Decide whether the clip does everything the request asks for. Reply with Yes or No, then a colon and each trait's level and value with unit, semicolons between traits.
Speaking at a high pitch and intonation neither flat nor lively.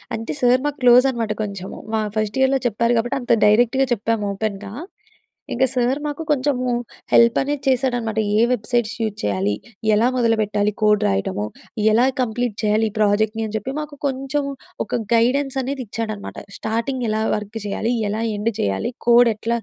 Yes: high, 230 Hz; average, 3.1 semitones